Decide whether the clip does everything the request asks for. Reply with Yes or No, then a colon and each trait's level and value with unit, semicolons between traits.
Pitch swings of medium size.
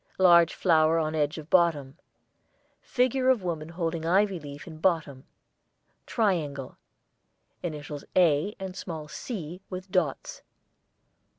Yes: average, 3.4 semitones